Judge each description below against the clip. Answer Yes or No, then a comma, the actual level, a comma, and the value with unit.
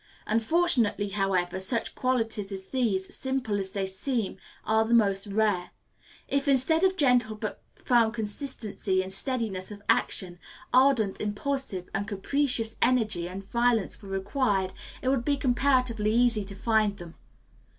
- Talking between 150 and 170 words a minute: No, average, 140 wpm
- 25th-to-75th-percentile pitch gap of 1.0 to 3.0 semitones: No, average, 4.4 semitones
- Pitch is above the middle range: Yes, high, 220 Hz